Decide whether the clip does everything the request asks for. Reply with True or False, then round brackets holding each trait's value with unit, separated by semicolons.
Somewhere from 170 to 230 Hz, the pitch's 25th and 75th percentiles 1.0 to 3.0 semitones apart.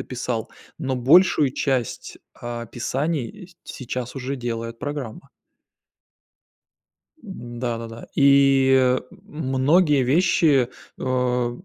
False (130 Hz; 2.6 semitones)